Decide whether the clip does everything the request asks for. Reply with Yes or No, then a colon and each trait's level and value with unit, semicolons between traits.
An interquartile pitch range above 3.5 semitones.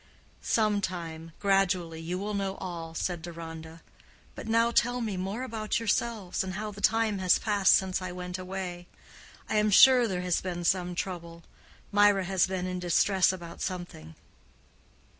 No: average, 2.9 semitones